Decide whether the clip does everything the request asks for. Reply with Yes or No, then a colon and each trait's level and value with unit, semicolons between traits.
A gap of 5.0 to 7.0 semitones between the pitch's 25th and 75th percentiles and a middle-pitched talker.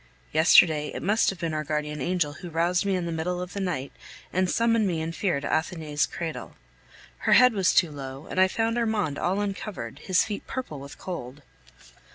No: average, 4.2 semitones; medium, 175 Hz